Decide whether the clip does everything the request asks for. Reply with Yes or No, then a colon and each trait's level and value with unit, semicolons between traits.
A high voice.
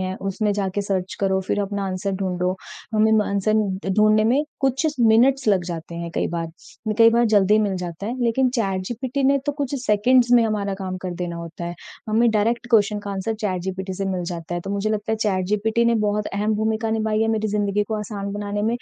Yes: high, 205 Hz